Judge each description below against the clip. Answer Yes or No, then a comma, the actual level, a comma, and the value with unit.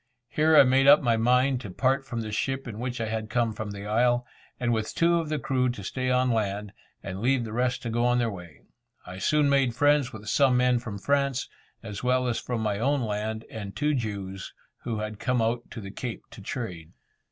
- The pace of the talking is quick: Yes, fast, 230 wpm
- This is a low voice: Yes, low, 120 Hz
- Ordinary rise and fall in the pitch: Yes, average, 3.2 semitones